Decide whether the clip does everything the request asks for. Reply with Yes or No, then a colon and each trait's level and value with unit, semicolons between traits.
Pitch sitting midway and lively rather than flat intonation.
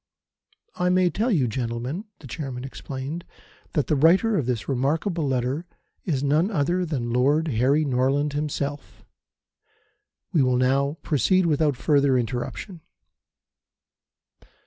No: medium, 145 Hz; average, 4.0 semitones